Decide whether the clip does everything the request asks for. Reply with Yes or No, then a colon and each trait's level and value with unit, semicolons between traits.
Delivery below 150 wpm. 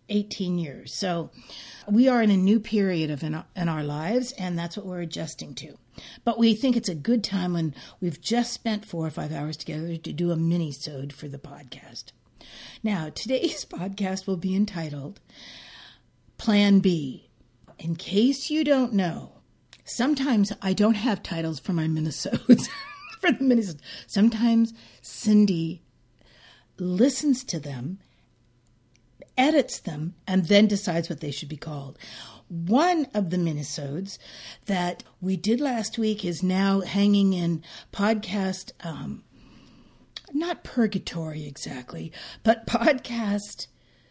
Yes: average, 140 wpm